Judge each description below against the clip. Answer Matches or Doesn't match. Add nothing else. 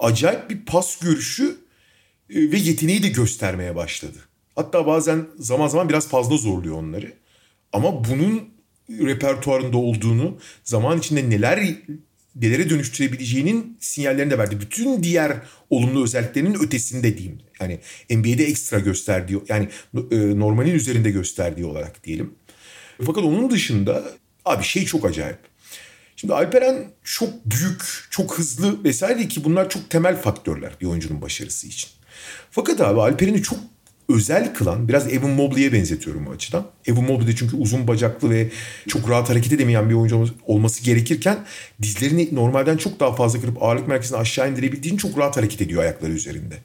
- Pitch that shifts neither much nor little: Doesn't match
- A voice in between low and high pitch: Doesn't match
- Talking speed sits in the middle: Doesn't match